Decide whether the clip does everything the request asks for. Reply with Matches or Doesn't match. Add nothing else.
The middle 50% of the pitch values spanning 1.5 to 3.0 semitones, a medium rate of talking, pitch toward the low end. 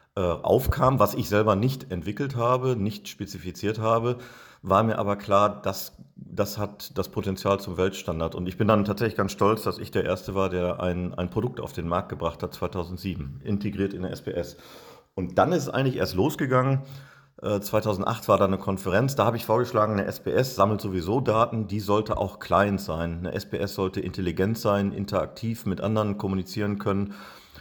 Matches